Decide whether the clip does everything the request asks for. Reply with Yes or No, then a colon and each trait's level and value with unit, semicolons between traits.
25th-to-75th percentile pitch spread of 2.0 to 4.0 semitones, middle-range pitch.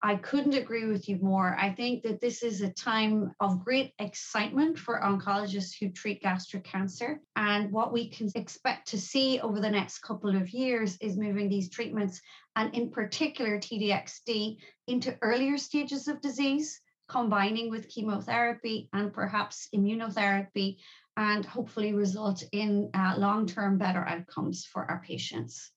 No: average, 2.8 semitones; high, 210 Hz